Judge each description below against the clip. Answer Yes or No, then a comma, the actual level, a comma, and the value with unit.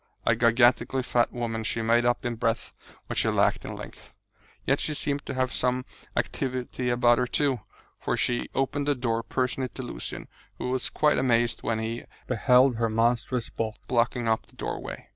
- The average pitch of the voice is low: Yes, low, 120 Hz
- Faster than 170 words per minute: Yes, average, 180 wpm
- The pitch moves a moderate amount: No, narrow, 1.7 semitones